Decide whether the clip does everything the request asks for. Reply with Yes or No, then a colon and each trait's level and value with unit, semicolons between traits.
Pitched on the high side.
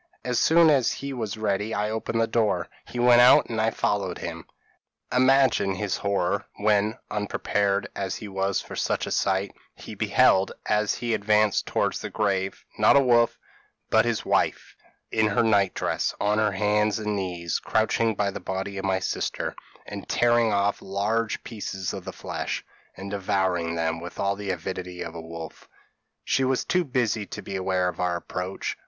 No: low, 100 Hz